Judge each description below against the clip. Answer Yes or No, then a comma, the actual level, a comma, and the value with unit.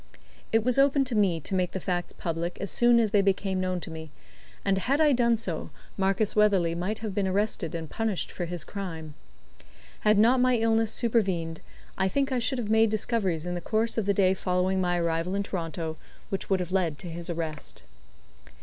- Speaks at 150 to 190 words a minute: No, fast, 205 wpm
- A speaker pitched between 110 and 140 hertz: No, high, 195 Hz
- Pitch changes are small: No, average, 4.3 semitones